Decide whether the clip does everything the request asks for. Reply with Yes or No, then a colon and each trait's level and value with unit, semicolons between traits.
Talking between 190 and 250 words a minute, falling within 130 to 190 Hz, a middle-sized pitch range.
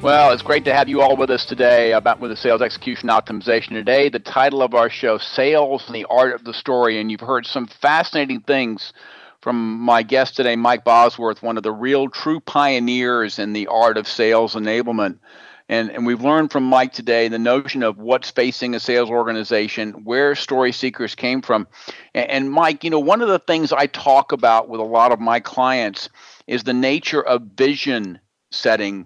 No: average, 200 wpm; low, 120 Hz; average, 3.0 semitones